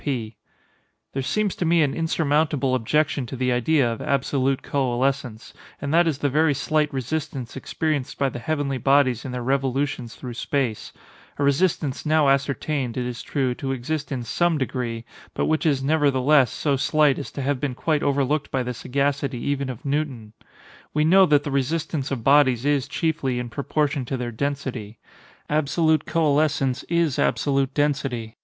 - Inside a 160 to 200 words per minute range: Yes, average, 165 wpm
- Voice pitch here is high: No, medium, 140 Hz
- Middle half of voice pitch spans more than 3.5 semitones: No, average, 2.8 semitones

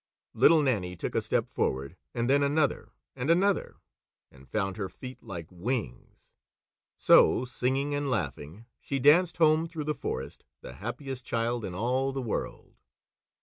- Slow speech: No, average, 150 wpm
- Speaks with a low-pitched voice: Yes, low, 125 Hz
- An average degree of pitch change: No, wide, 6.4 semitones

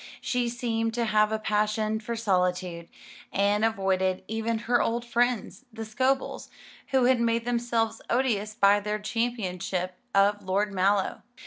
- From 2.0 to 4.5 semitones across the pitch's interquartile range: Yes, average, 2.8 semitones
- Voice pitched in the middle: No, high, 220 Hz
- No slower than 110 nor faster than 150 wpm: Yes, average, 140 wpm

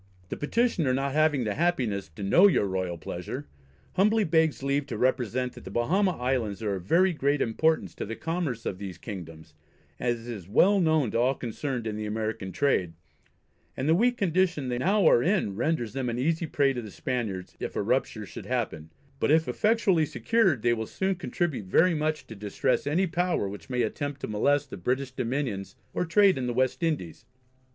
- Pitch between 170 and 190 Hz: No, low, 130 Hz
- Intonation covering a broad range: Yes, wide, 6.9 semitones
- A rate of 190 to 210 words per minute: Yes, average, 195 wpm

